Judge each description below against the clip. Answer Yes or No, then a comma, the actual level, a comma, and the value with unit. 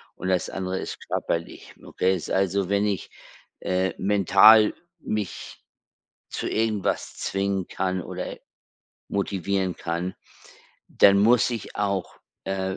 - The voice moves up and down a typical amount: No, narrow, 1.4 semitones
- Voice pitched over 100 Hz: No, very low, 95 Hz